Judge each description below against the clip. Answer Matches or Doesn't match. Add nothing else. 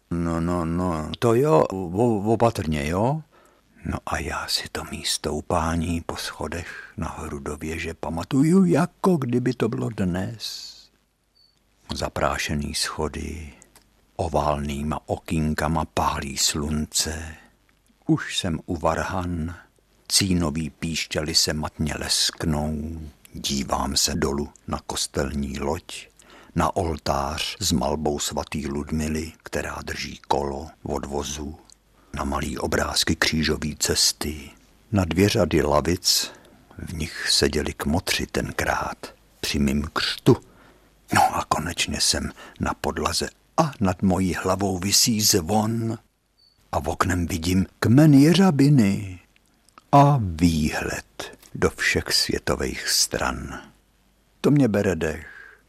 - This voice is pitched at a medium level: Doesn't match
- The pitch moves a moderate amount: Matches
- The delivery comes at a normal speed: Doesn't match